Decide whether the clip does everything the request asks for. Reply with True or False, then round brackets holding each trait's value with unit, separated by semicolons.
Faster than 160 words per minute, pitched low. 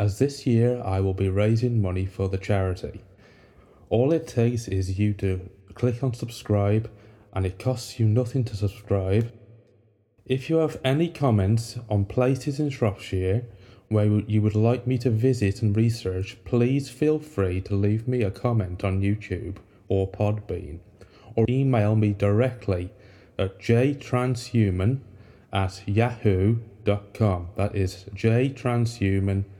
False (140 wpm; 105 Hz)